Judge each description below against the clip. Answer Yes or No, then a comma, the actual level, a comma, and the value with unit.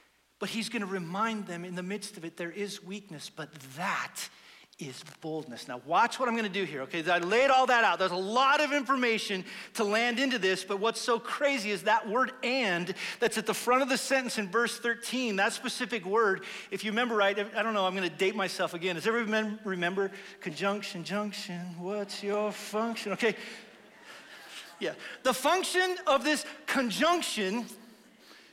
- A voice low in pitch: No, high, 210 Hz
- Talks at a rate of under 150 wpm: No, average, 190 wpm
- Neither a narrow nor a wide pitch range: Yes, average, 4.0 semitones